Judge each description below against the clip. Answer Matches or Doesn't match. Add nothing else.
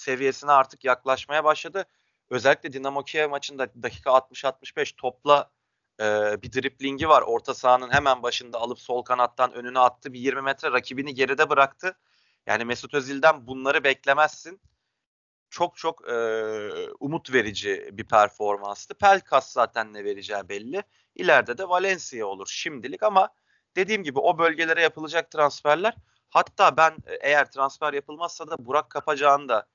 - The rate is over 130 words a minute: Matches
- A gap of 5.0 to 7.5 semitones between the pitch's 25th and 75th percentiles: Doesn't match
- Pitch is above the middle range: Doesn't match